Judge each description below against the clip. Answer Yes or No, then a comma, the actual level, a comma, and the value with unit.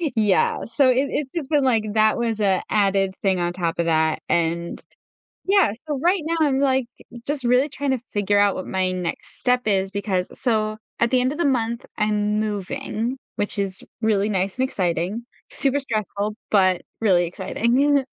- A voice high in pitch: Yes, high, 215 Hz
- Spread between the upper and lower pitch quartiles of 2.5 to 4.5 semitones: No, wide, 5.4 semitones